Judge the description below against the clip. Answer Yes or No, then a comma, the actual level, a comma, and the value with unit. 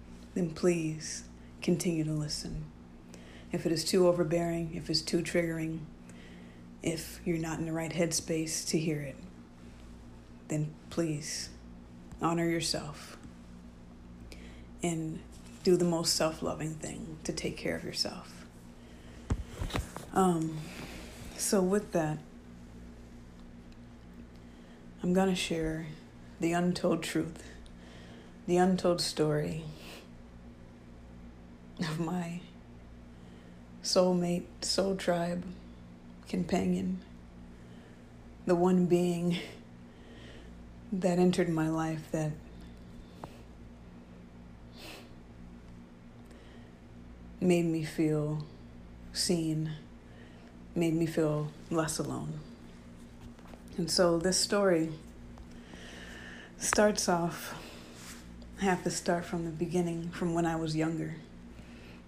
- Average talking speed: No, slow, 90 wpm